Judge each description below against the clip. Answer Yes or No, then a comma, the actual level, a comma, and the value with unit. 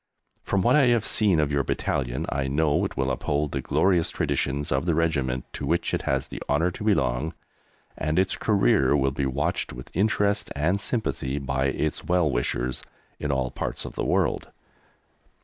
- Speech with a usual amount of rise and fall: Yes, average, 5.0 semitones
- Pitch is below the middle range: Yes, very low, 75 Hz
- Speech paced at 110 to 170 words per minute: No, average, 185 wpm